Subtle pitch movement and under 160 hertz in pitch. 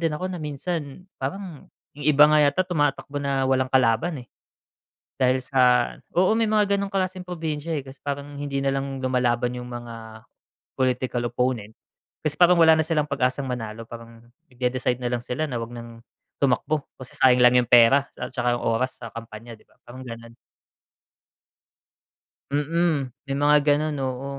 No: average, 3.5 semitones; low, 135 Hz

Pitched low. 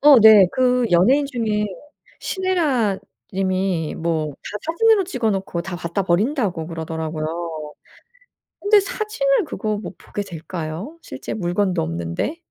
No: high, 205 Hz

